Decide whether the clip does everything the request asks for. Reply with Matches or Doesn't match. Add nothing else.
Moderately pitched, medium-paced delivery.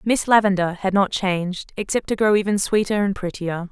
Doesn't match